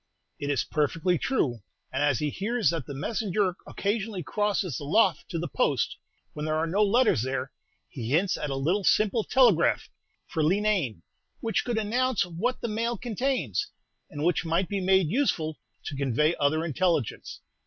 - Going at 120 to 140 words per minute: No, average, 170 wpm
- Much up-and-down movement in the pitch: Yes, wide, 6.3 semitones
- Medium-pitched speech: Yes, medium, 175 Hz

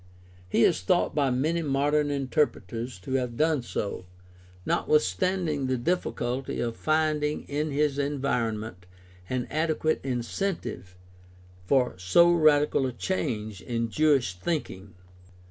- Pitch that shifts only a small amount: No, average, 4.6 semitones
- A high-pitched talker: No, low, 135 Hz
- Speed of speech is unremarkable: No, slow, 115 wpm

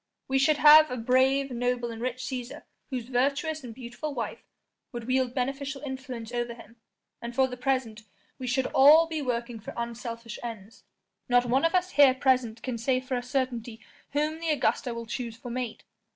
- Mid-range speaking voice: No, very high, 255 Hz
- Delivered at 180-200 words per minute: Yes, average, 185 wpm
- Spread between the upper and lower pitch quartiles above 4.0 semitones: No, narrow, 2.4 semitones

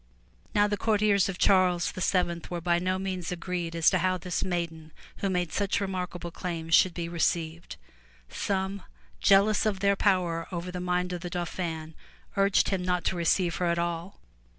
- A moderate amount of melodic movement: No, narrow, 1.9 semitones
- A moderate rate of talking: Yes, average, 175 wpm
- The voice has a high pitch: No, medium, 180 Hz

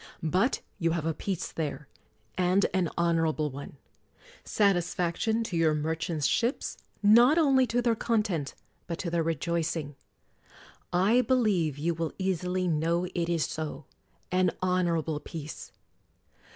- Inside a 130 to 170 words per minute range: Yes, average, 140 wpm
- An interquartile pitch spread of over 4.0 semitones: No, average, 3.5 semitones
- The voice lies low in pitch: No, medium, 170 Hz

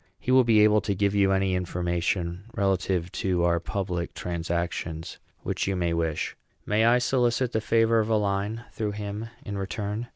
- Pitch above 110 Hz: No, low, 100 Hz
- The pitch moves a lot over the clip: No, average, 3.8 semitones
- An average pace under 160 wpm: No, average, 175 wpm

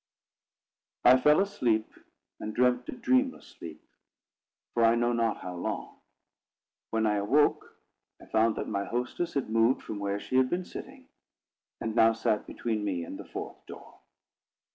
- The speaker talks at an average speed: Yes, average, 160 wpm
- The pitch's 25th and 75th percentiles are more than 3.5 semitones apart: No, average, 3.1 semitones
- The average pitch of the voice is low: Yes, low, 115 Hz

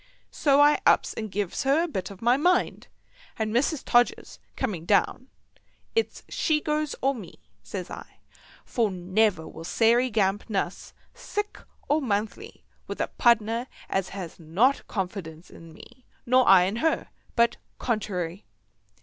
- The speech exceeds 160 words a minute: No, average, 150 wpm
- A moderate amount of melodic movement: No, wide, 5.9 semitones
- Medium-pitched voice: No, high, 220 Hz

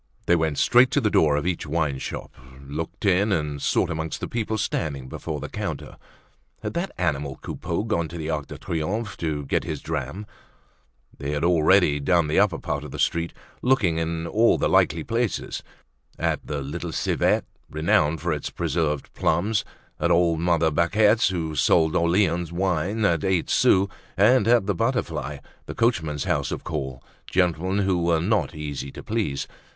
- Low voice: Yes, very low, 85 Hz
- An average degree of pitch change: Yes, average, 4.3 semitones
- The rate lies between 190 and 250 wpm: No, average, 175 wpm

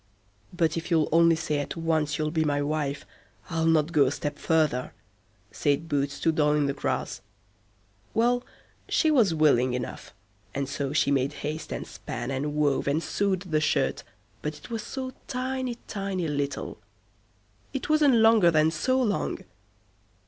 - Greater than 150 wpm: Yes, average, 160 wpm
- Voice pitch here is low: No, medium, 155 Hz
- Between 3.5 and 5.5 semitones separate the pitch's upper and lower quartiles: Yes, average, 4.7 semitones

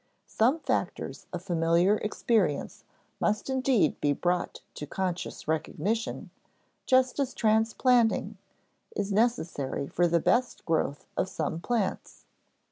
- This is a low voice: No, high, 205 Hz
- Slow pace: Yes, slow, 115 wpm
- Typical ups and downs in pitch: No, wide, 6.2 semitones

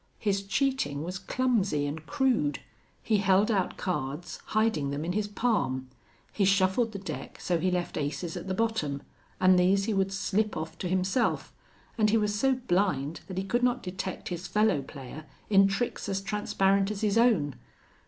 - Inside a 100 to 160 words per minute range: No, average, 180 wpm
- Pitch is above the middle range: Yes, high, 195 Hz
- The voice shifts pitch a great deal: No, average, 3.5 semitones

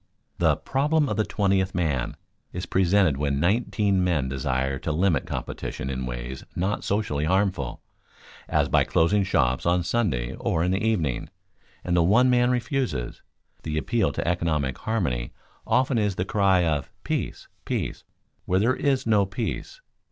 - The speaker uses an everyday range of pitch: No, wide, 6.7 semitones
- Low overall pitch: Yes, very low, 90 Hz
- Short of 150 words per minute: No, average, 155 wpm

